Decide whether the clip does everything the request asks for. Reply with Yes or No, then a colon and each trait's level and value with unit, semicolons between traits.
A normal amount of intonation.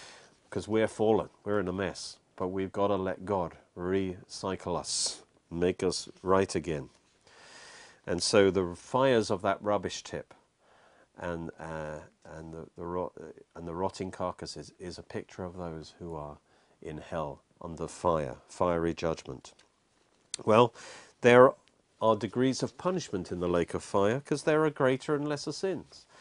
Yes: average, 4.3 semitones